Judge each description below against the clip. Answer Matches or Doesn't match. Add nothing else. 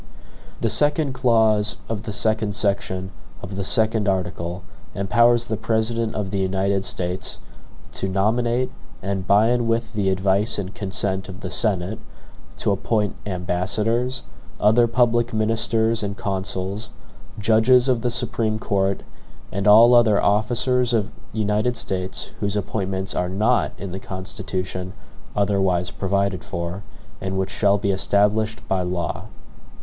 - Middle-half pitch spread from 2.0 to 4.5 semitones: Matches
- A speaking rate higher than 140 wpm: Doesn't match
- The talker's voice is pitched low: Matches